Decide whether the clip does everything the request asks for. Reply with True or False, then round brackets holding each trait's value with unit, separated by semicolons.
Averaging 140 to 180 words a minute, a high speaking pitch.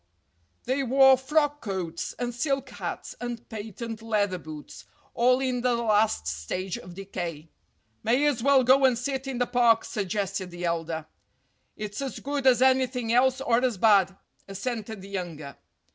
True (160 wpm; 230 Hz)